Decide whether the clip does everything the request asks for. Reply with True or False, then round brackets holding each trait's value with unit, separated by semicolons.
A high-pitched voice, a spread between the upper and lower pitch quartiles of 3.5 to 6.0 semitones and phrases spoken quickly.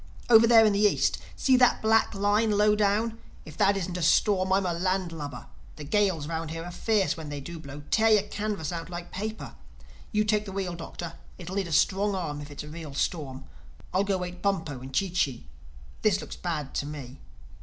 False (180 Hz; 4.6 semitones; 210 wpm)